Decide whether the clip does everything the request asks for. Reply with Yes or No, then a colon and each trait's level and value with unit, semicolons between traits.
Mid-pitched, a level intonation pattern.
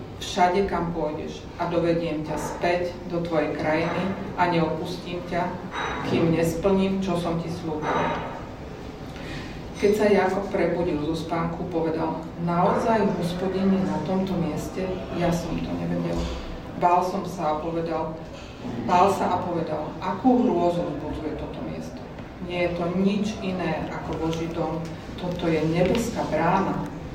Yes: medium, 175 Hz; narrow, 2.2 semitones